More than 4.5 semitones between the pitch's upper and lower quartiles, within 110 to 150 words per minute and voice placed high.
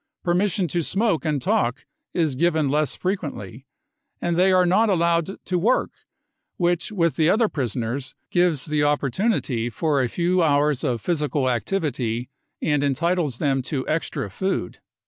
No: average, 4.9 semitones; average, 145 wpm; medium, 155 Hz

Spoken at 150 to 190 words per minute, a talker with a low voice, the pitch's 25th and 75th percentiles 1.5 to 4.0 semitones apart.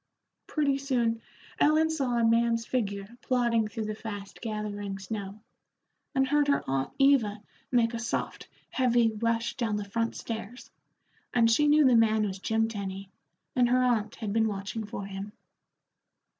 No: average, 155 wpm; high, 225 Hz; average, 2.9 semitones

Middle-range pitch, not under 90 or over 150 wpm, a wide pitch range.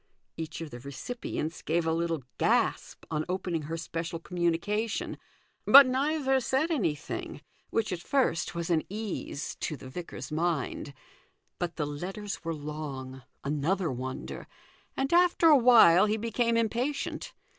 Yes: medium, 170 Hz; average, 140 wpm; wide, 6.9 semitones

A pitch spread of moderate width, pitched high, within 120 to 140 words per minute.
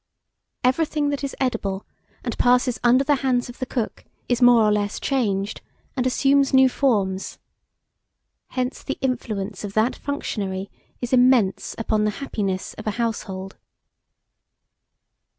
Yes: average, 4.2 semitones; high, 240 Hz; slow, 135 wpm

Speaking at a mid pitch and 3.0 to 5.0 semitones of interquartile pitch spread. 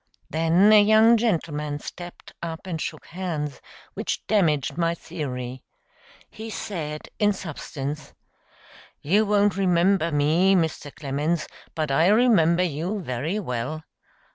Yes: medium, 170 Hz; average, 4.6 semitones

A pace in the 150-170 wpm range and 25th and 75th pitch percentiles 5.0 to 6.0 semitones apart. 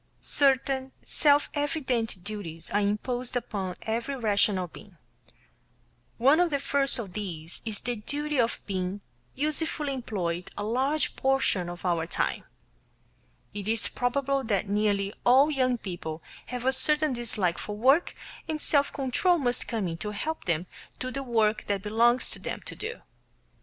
Yes: average, 155 wpm; average, 5.3 semitones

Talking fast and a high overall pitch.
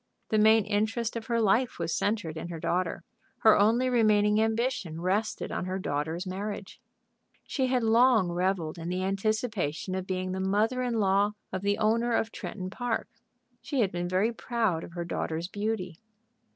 No: average, 175 wpm; high, 205 Hz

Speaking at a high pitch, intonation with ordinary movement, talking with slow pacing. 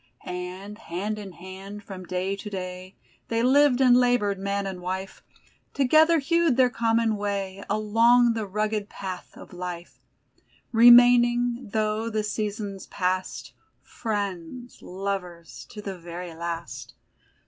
Yes: high, 205 Hz; average, 3.9 semitones; slow, 125 wpm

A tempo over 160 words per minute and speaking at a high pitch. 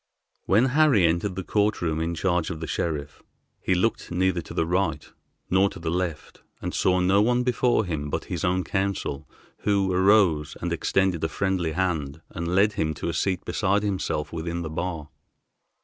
No: average, 185 wpm; very low, 90 Hz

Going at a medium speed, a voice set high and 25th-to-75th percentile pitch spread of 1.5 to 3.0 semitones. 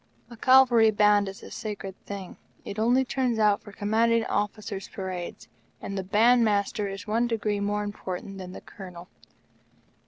Yes: average, 160 wpm; high, 205 Hz; narrow, 2.4 semitones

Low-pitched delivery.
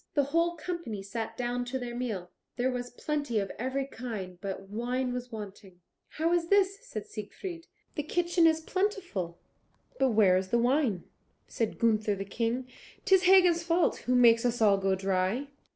No: high, 245 Hz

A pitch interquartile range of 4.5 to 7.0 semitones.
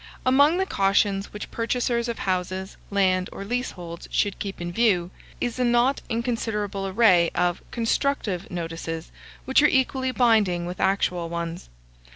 Yes: average, 5.1 semitones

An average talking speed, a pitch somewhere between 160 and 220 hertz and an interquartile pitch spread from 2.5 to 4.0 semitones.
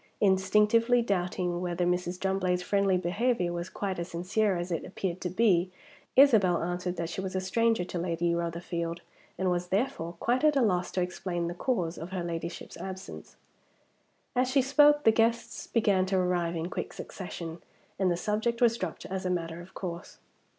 Yes: average, 180 wpm; medium, 185 Hz; average, 3.4 semitones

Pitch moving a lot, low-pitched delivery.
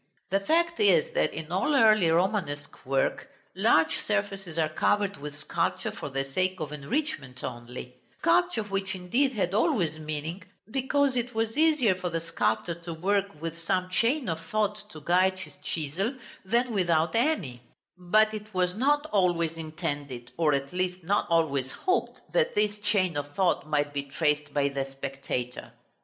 No: wide, 6.1 semitones; medium, 180 Hz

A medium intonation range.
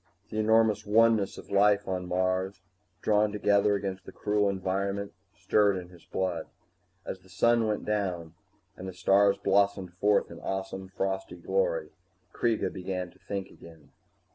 No: narrow, 2.0 semitones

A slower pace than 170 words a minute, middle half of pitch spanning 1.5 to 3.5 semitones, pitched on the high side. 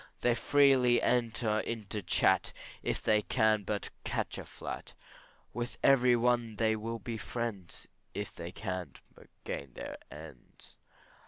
No: average, 140 wpm; average, 2.8 semitones; low, 110 Hz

